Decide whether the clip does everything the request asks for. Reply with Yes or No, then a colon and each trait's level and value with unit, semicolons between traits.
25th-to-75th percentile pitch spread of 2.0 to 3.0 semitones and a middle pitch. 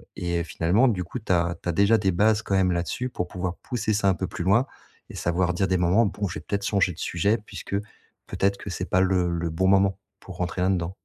No: narrow, 2.4 semitones; very low, 95 Hz